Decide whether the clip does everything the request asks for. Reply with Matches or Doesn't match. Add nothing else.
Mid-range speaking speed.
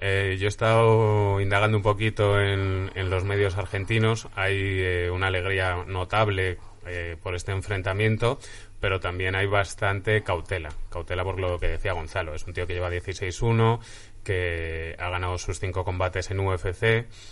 Matches